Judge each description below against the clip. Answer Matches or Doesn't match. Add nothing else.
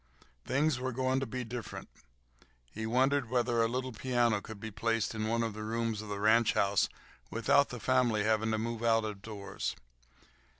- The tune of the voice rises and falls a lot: Doesn't match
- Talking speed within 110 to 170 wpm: Doesn't match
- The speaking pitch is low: Matches